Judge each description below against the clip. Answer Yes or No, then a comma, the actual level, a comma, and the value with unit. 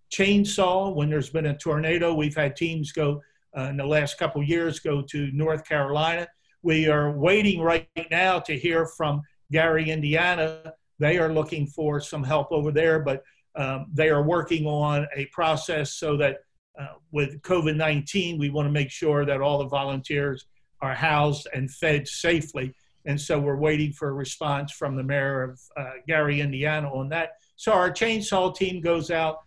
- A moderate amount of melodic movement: No, narrow, 2.3 semitones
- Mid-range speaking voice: Yes, medium, 150 Hz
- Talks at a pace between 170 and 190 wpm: Yes, average, 180 wpm